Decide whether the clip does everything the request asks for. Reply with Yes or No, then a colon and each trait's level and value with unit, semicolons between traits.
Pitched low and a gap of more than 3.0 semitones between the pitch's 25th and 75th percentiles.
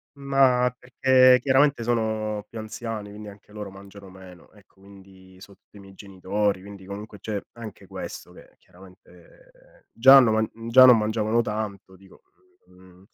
Yes: low, 105 Hz; average, 3.7 semitones